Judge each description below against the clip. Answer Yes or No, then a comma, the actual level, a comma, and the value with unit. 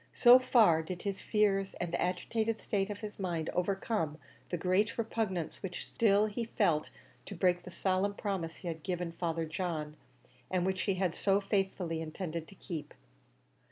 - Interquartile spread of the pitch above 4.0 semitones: No, average, 3.2 semitones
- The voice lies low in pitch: No, medium, 185 Hz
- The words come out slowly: No, average, 170 wpm